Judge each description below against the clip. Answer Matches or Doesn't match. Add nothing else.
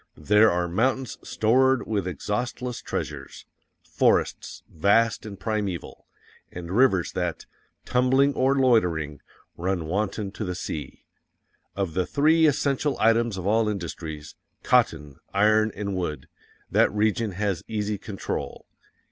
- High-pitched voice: Doesn't match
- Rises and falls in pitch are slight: Doesn't match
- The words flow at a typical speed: Doesn't match